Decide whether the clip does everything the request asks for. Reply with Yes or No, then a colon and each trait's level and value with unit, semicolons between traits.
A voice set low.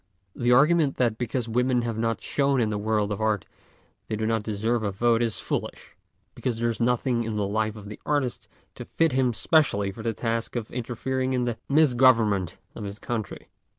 Yes: low, 115 Hz